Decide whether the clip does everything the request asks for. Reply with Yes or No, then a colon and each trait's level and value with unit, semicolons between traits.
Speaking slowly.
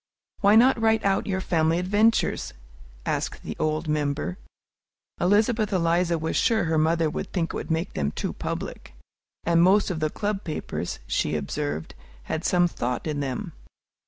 No: average, 160 wpm